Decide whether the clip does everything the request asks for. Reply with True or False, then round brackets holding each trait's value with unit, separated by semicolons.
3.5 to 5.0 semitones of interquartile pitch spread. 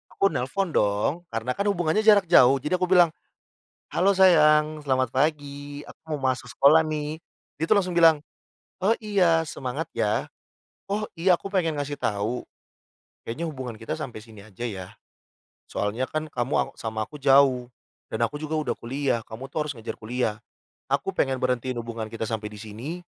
False (5.4 semitones)